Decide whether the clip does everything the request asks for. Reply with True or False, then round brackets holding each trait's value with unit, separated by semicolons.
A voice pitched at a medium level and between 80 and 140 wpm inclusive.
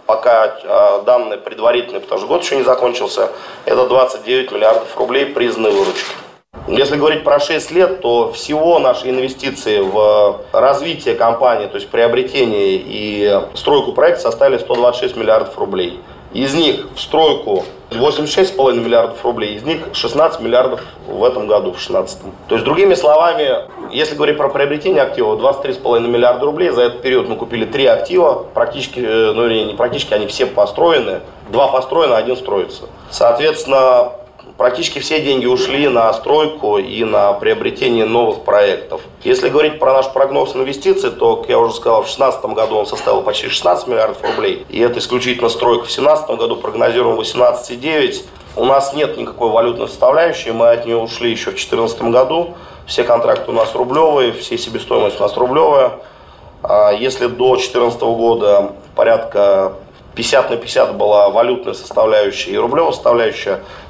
False (150 Hz; 150 wpm)